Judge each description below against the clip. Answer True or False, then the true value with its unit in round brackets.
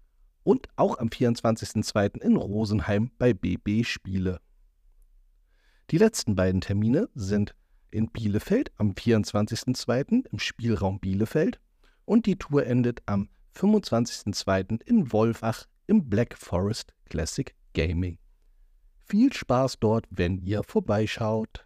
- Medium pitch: False (110 Hz)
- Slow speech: True (110 wpm)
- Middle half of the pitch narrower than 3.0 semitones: False (4.3 semitones)